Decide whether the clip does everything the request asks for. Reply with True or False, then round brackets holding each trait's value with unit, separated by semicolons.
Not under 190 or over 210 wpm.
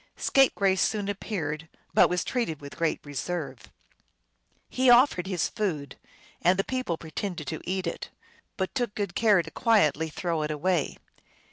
False (150 wpm)